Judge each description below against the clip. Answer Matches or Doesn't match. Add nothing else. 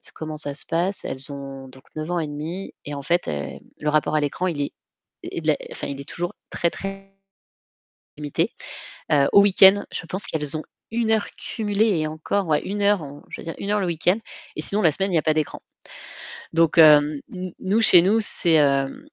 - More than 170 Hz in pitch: Doesn't match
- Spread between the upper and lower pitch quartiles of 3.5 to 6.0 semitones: Matches